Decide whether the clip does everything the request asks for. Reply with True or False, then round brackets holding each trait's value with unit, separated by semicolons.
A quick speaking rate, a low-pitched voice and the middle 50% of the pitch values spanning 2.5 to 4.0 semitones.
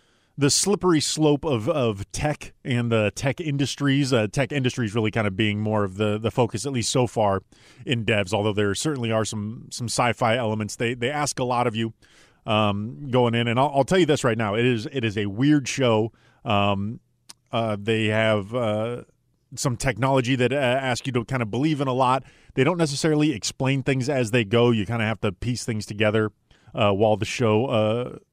True (215 wpm; 120 Hz; 3.7 semitones)